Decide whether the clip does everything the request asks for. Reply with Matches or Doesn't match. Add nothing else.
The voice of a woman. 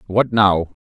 Doesn't match